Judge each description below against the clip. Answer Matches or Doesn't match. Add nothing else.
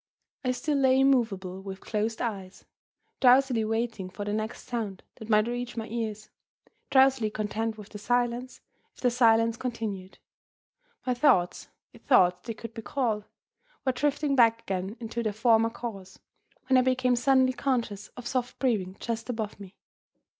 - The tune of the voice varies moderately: Matches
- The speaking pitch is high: Matches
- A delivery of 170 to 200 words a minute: Doesn't match